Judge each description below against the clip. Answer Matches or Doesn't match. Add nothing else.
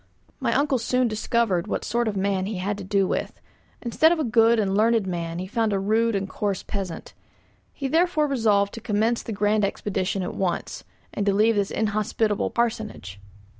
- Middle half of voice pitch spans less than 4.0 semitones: Matches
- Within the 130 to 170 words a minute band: Doesn't match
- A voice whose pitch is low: Doesn't match